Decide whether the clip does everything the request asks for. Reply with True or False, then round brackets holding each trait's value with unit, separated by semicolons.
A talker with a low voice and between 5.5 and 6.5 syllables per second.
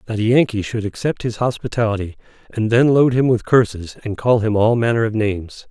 True (110 Hz; 5.7 syllables/s)